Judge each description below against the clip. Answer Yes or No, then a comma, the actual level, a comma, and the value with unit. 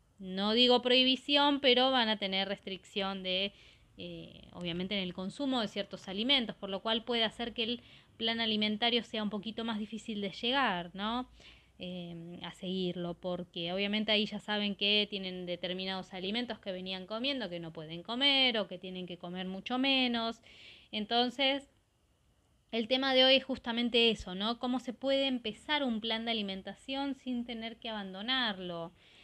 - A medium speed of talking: Yes, average, 165 wpm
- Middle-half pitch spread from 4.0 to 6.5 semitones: Yes, average, 4.4 semitones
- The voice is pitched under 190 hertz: No, high, 215 Hz